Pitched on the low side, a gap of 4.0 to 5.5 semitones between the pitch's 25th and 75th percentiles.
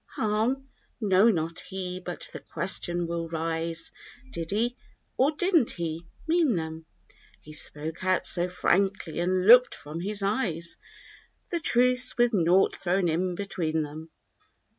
No: medium, 185 Hz; average, 4.8 semitones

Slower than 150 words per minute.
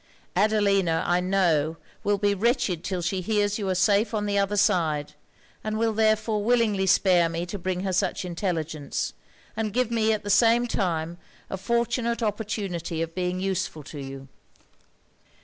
No: average, 165 wpm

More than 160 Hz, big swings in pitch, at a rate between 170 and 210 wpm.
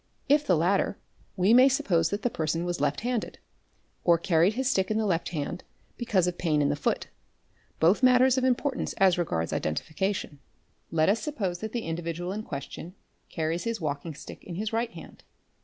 Yes: medium, 185 Hz; wide, 5.7 semitones; average, 195 wpm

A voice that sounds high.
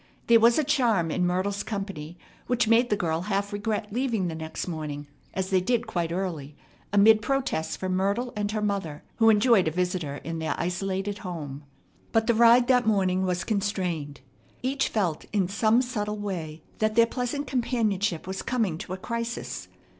Yes: high, 200 Hz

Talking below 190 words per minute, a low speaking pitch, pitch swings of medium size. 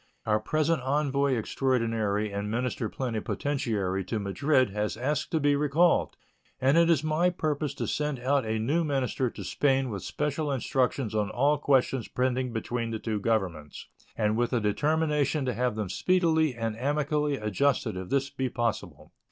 Yes: average, 165 wpm; low, 130 Hz; average, 4.8 semitones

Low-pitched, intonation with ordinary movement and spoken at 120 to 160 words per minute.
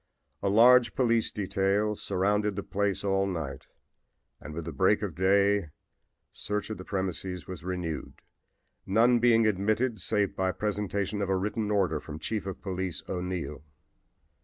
No: low, 100 Hz; narrow, 2.3 semitones; average, 150 wpm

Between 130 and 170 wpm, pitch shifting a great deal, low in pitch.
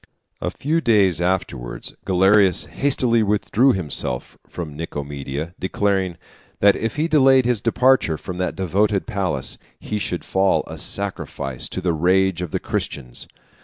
No: average, 140 wpm; average, 4.3 semitones; very low, 95 Hz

